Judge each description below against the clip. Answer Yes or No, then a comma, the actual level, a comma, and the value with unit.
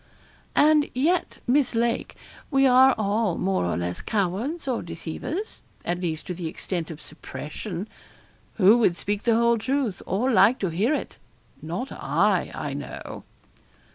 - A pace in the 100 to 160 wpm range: Yes, average, 150 wpm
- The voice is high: Yes, high, 215 Hz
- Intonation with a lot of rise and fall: Yes, wide, 6.6 semitones